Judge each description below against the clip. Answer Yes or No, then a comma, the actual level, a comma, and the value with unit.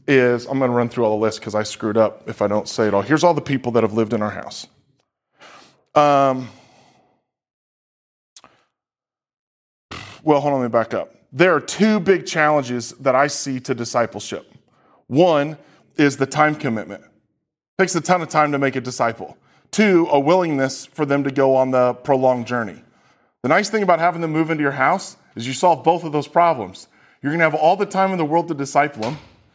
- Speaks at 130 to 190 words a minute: No, fast, 205 wpm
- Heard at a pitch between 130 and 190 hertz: Yes, medium, 140 Hz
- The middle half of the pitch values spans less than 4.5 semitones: No, average, 5.0 semitones